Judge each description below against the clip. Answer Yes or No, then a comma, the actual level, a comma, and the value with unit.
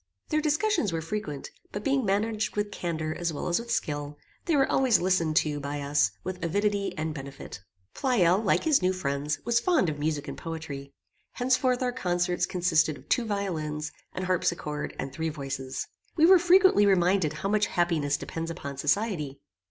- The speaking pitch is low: No, medium, 175 Hz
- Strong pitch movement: Yes, wide, 6.0 semitones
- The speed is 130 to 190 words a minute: Yes, average, 175 wpm